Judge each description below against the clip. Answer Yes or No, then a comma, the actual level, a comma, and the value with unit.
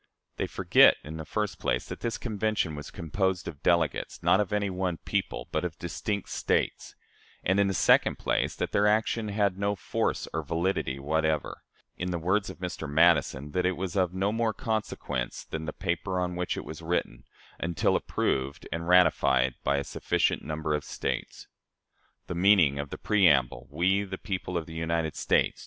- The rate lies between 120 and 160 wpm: No, average, 185 wpm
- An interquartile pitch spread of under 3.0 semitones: No, average, 3.9 semitones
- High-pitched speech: No, very low, 90 Hz